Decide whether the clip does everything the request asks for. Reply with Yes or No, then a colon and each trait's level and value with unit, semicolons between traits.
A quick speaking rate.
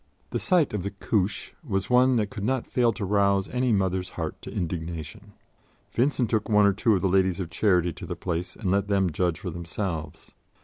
Yes: fast, 210 wpm